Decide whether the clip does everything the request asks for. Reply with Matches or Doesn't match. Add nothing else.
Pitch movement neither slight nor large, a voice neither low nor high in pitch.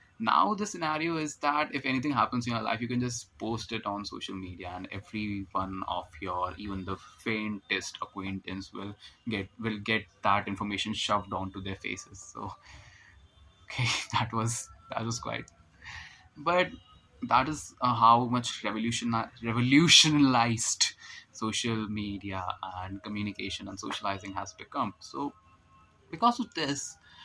Doesn't match